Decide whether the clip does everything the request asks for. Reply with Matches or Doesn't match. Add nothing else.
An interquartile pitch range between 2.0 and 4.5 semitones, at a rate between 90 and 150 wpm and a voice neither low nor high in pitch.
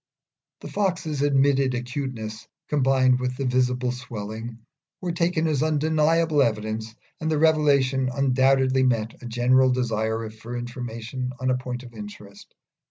Doesn't match